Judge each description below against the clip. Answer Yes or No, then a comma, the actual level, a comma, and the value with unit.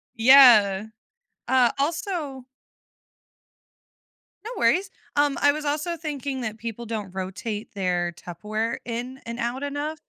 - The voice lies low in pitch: No, high, 245 Hz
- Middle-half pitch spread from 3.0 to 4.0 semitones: No, average, 5.1 semitones